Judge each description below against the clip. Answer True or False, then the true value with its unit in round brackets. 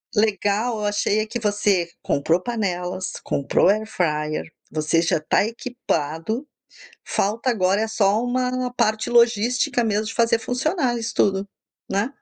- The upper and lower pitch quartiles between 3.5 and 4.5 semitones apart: True (4.1 semitones)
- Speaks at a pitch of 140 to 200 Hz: False (215 Hz)